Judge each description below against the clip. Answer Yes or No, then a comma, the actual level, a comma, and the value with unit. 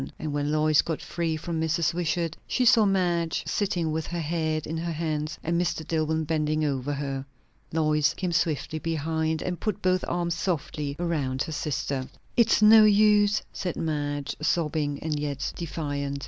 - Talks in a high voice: No, medium, 160 Hz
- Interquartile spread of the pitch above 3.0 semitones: No, narrow, 2.4 semitones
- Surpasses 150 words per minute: Yes, average, 165 wpm